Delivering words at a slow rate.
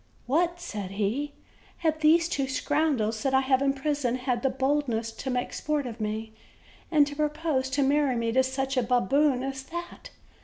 No: average, 185 wpm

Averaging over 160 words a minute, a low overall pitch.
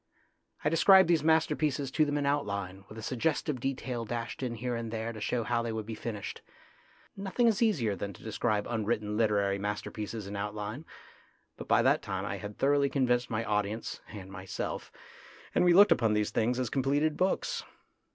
Yes: average, 185 wpm; low, 115 Hz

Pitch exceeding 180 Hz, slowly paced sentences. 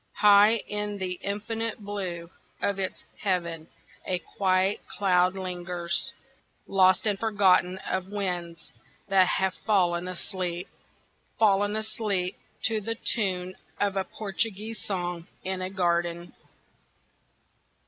Yes: high, 190 Hz; slow, 110 wpm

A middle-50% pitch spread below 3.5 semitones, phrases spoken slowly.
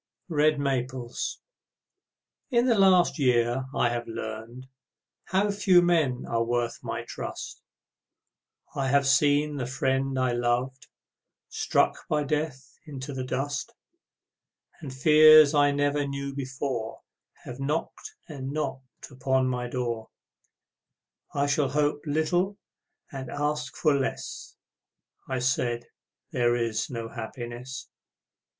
Yes: average, 3.1 semitones; slow, 120 wpm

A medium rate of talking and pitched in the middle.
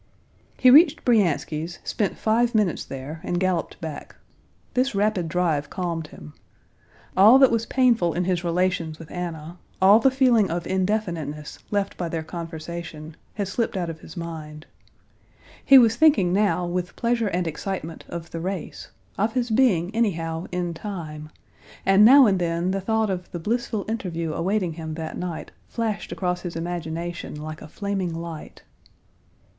Yes: average, 160 wpm; medium, 180 Hz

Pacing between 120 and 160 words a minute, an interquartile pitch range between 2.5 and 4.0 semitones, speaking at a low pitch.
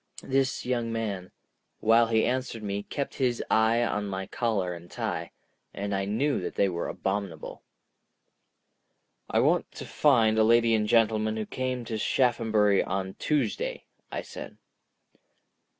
Yes: average, 140 wpm; average, 2.9 semitones; low, 110 Hz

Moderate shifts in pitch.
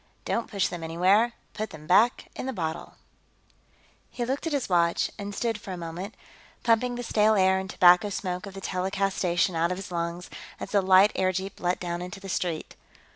Yes: average, 3.0 semitones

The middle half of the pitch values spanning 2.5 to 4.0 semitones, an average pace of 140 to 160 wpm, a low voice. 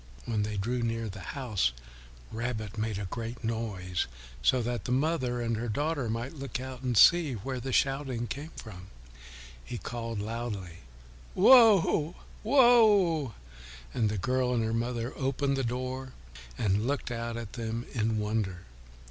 Yes: average, 3.4 semitones; average, 155 wpm; low, 120 Hz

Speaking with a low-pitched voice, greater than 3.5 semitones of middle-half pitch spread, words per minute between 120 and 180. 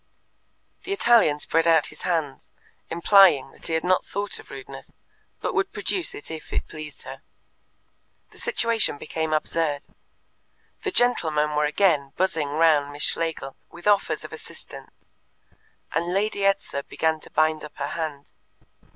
No: medium, 160 Hz; average, 4.7 semitones; average, 150 wpm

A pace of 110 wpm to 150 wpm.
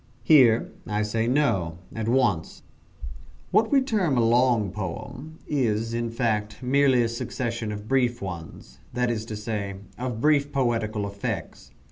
Yes: average, 145 wpm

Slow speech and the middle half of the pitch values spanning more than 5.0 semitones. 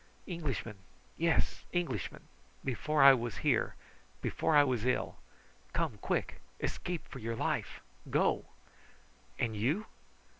Yes: slow, 115 wpm; wide, 5.6 semitones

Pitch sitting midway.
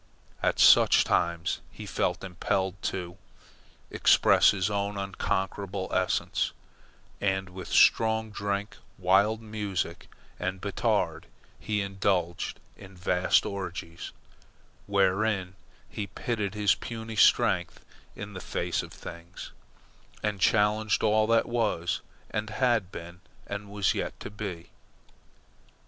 No: low, 100 Hz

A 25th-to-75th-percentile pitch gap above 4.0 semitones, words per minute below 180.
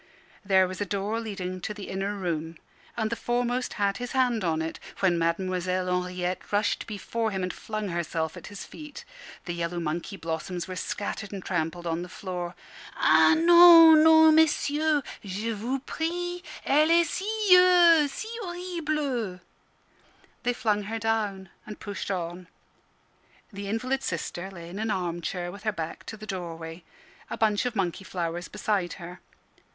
Yes: average, 5.2 semitones; average, 160 wpm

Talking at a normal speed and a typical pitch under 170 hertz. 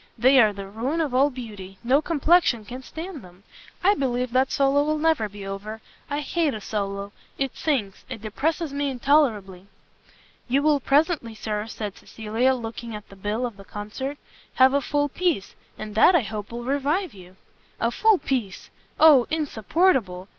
No: average, 175 wpm; very high, 250 Hz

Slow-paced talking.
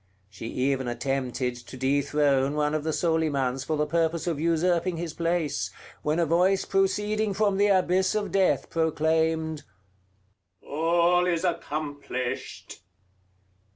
Yes: slow, 125 wpm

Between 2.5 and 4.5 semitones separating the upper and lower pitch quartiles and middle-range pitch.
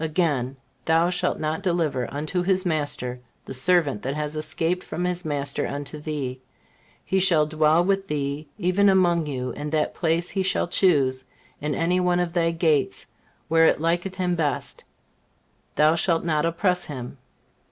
Yes: average, 3.3 semitones; medium, 160 Hz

